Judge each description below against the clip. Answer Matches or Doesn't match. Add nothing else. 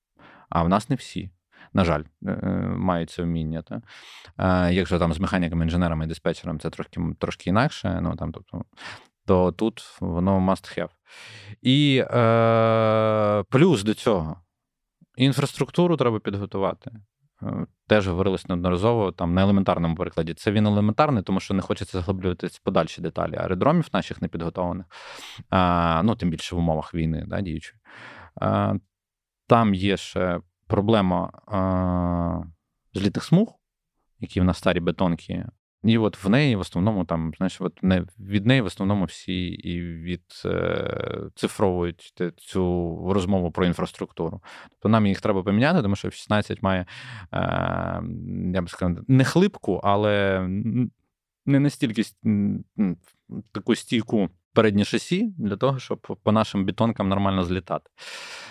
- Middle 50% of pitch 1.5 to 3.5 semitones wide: Doesn't match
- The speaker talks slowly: Doesn't match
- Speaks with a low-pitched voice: Matches